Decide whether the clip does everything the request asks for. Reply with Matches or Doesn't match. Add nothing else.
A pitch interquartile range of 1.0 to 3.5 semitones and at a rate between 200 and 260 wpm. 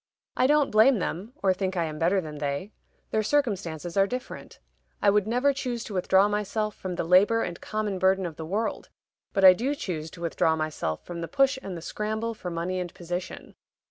Doesn't match